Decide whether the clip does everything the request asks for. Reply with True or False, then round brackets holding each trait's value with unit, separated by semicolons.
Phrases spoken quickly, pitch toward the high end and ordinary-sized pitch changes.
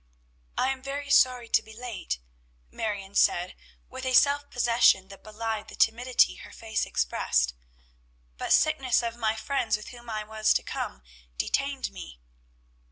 False (155 wpm; 230 Hz; 3.6 semitones)